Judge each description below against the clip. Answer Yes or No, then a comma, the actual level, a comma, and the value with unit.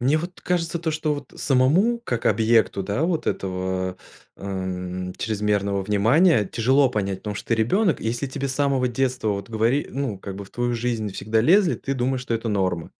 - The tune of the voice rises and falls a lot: Yes, wide, 5.7 semitones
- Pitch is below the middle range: Yes, low, 115 Hz